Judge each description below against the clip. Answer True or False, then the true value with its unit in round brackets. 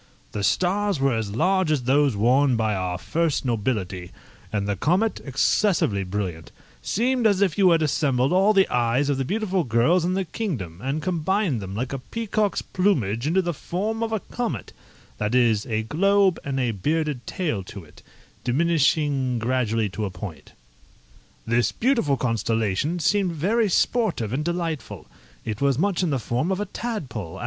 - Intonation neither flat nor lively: False (8.5 semitones)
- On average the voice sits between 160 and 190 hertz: False (140 Hz)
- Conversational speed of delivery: True (170 wpm)